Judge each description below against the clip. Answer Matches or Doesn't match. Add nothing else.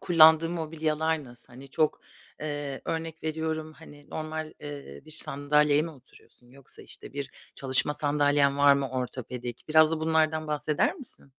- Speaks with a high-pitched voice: Doesn't match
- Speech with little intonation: Matches